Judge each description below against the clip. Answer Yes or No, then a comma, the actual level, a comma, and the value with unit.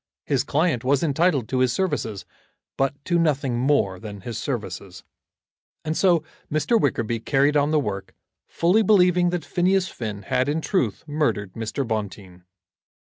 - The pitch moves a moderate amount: No, wide, 6.8 semitones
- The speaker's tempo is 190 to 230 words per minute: No, average, 150 wpm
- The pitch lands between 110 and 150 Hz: Yes, low, 135 Hz